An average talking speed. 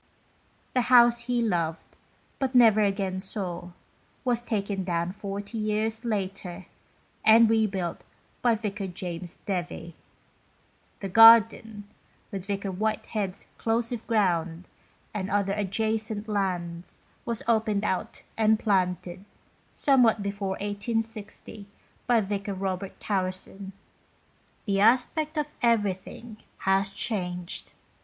No: slow, 115 wpm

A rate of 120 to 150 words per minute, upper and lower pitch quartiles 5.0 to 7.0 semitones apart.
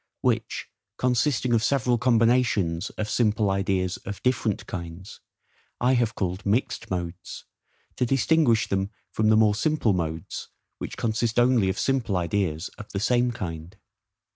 No: average, 140 wpm; average, 4.4 semitones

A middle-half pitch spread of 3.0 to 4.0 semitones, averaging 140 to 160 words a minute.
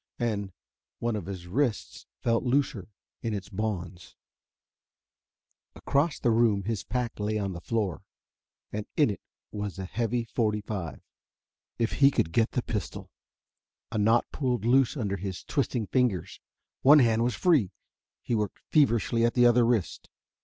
Yes: average, 3.3 semitones; average, 155 wpm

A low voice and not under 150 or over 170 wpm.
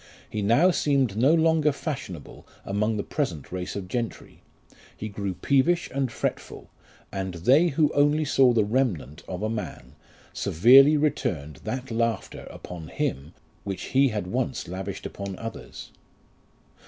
No: low, 115 Hz; average, 140 wpm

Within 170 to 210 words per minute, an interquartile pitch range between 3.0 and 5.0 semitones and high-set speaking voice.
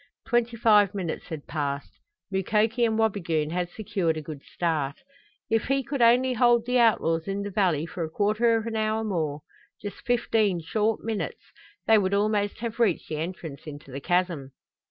No: average, 175 wpm; wide, 5.4 semitones; high, 205 Hz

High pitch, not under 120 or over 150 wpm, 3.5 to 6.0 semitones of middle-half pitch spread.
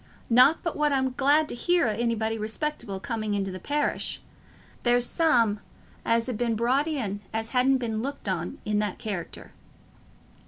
No: high, 235 Hz; average, 165 wpm; average, 4.2 semitones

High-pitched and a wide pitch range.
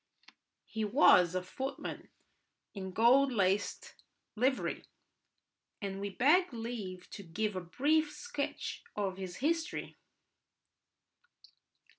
Yes: high, 215 Hz; wide, 6.4 semitones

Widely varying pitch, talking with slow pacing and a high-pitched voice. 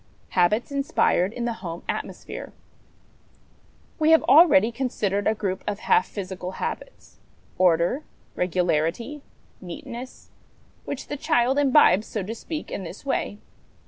Yes: wide, 6.7 semitones; slow, 125 wpm; high, 215 Hz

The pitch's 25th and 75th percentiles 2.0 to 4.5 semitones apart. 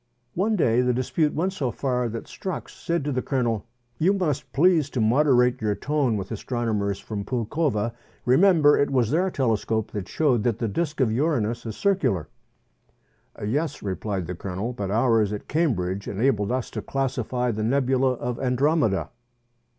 No: average, 5.2 semitones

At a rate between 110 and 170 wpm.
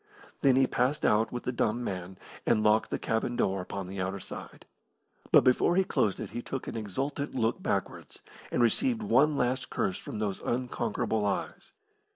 No: average, 185 wpm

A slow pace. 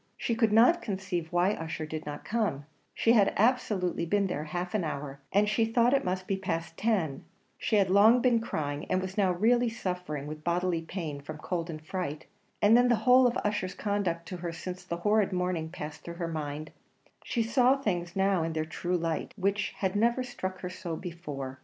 No: fast, 205 wpm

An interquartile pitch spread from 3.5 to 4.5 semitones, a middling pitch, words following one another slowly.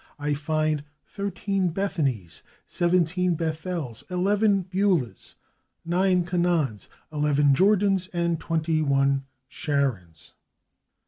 Yes: average, 4.2 semitones; medium, 165 Hz; slow, 85 wpm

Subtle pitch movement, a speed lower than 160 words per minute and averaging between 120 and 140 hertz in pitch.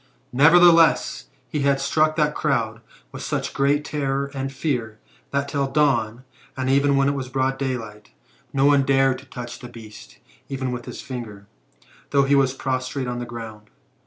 No: narrow, 2.2 semitones; average, 175 wpm; low, 135 Hz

